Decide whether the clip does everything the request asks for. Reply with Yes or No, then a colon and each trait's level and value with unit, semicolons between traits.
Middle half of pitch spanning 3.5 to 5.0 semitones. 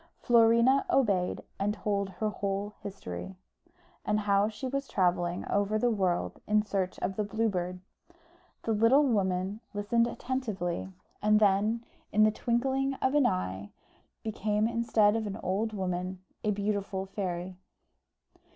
No: average, 3.1 semitones